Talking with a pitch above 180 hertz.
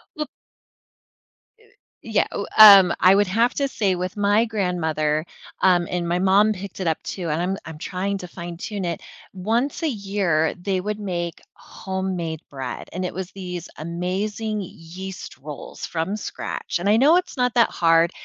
Yes: high, 190 Hz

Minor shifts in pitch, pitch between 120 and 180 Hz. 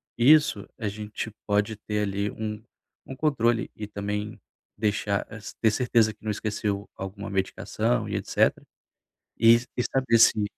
No: narrow, 2.0 semitones; low, 105 Hz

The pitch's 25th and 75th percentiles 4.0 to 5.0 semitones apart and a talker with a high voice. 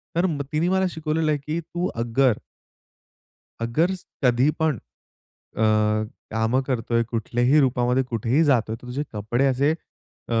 No: average, 4.7 semitones; low, 130 Hz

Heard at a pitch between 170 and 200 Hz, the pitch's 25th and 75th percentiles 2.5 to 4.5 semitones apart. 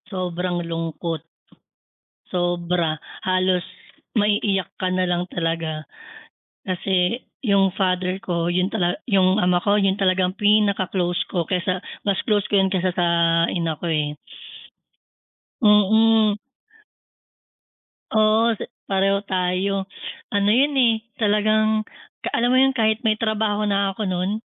Yes: high, 190 Hz; average, 2.8 semitones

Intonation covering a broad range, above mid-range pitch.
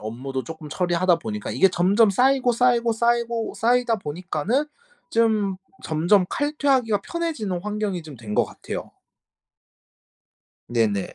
Yes: wide, 6.0 semitones; high, 205 Hz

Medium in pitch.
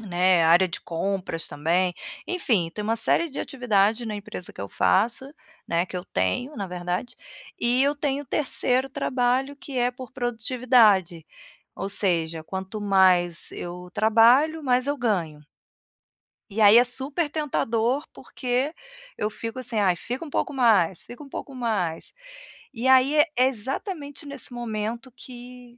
No: high, 235 Hz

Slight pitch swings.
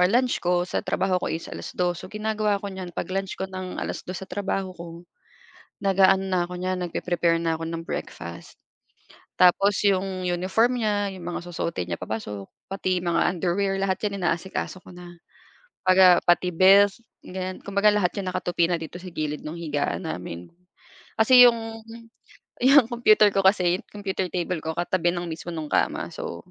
Yes: narrow, 2.2 semitones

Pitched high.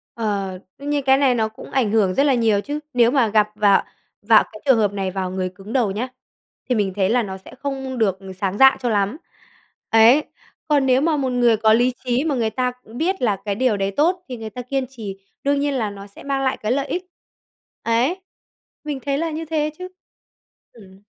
Yes: high, 240 Hz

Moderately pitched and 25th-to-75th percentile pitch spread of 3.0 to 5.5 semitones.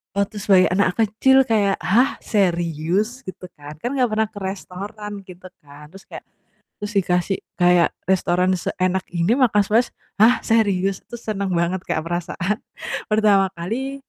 No: high, 195 Hz; average, 3.3 semitones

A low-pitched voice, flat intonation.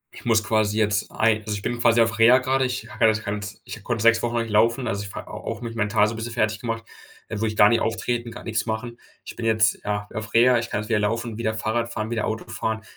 Yes: low, 110 Hz; narrow, 1.5 semitones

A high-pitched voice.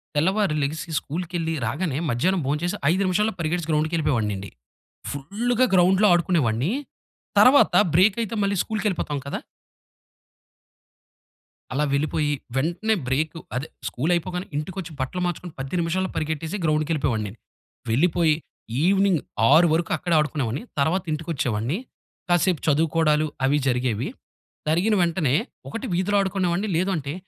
No: medium, 165 Hz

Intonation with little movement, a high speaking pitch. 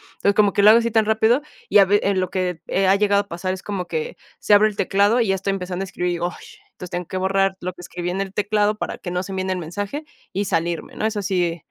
Yes: narrow, 2.3 semitones; high, 195 Hz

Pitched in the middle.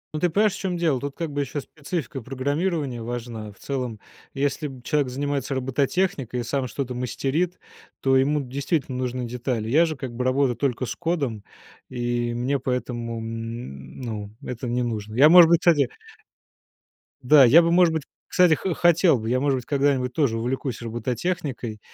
No: low, 130 Hz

